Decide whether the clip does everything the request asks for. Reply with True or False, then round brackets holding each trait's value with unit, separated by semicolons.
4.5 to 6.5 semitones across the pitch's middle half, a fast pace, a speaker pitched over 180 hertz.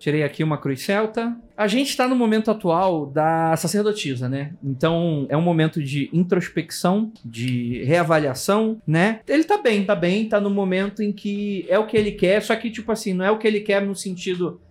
True (5.1 semitones; 205 wpm; 190 Hz)